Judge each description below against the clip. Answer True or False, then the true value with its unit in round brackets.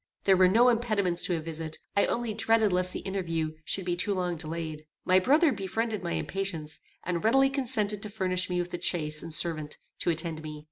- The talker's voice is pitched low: False (185 Hz)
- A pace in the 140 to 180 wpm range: False (205 wpm)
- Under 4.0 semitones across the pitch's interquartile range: False (4.3 semitones)